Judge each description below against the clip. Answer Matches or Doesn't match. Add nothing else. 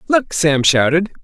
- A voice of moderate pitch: Matches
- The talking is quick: Doesn't match